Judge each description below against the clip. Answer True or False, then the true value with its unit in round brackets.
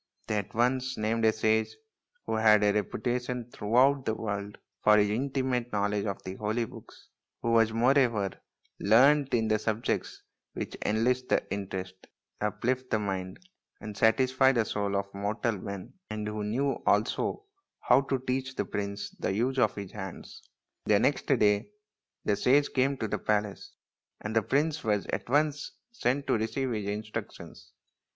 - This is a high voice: False (110 Hz)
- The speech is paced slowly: False (160 wpm)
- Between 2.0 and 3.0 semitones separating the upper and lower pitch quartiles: False (3.7 semitones)